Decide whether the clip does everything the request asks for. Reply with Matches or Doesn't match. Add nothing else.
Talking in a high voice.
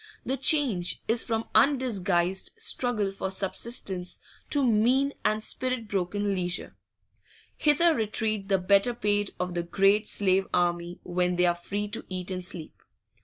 Matches